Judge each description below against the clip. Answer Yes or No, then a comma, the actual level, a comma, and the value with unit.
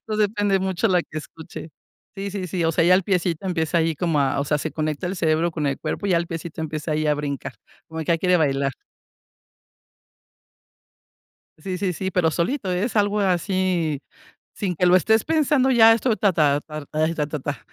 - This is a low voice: No, medium, 170 Hz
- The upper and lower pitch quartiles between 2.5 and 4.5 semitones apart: Yes, average, 3.9 semitones